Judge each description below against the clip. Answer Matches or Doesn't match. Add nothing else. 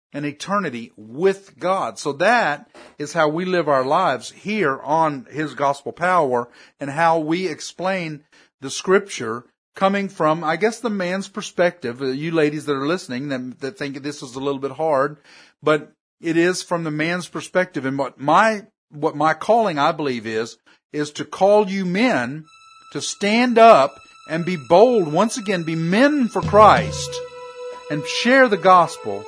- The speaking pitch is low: Doesn't match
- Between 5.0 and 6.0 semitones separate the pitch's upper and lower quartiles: Matches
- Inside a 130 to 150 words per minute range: Doesn't match